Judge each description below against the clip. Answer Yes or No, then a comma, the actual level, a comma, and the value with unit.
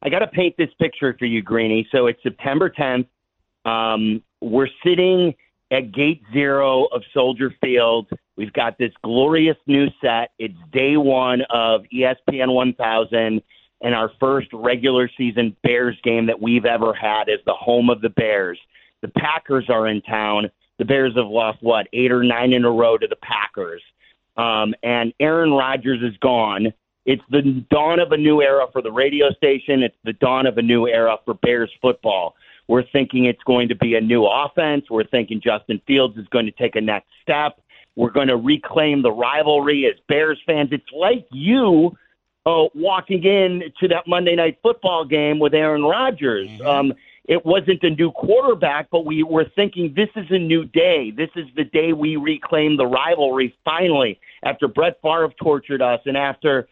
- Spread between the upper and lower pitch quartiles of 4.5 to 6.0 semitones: Yes, average, 5.1 semitones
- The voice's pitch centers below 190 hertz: Yes, low, 135 Hz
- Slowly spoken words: No, average, 180 wpm